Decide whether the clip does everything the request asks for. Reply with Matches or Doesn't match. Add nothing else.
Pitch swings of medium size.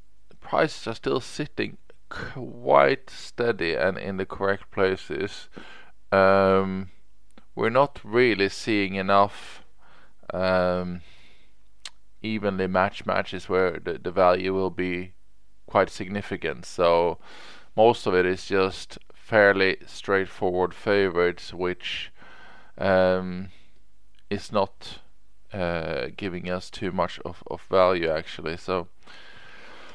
Doesn't match